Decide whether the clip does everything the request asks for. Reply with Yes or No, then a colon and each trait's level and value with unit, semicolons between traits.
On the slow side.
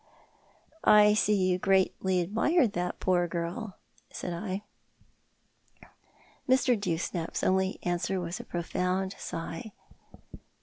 Yes: slow, 105 wpm